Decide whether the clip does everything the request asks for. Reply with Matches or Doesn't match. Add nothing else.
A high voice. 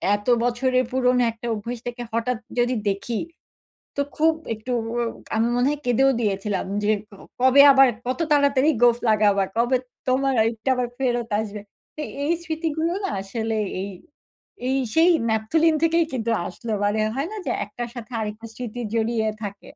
Matches